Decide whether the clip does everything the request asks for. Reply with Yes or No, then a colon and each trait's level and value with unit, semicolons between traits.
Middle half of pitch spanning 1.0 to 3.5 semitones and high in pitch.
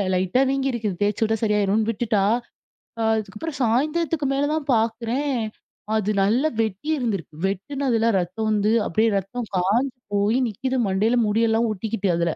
No: average, 3.9 semitones; high, 225 Hz